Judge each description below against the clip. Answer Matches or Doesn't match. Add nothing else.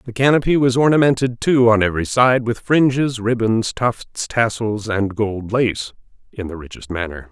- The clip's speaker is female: Doesn't match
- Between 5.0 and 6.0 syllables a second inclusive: Doesn't match